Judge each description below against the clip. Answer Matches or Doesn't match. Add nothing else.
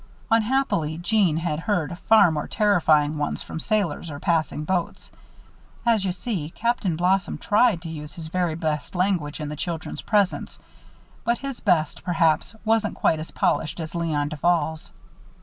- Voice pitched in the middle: Matches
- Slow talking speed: Doesn't match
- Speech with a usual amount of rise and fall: Matches